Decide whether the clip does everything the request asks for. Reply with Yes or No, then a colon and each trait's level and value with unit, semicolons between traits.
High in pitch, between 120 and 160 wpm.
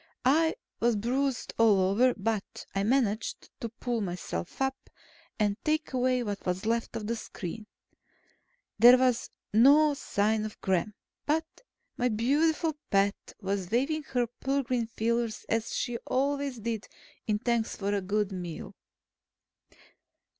Yes: high, 230 Hz; average, 140 wpm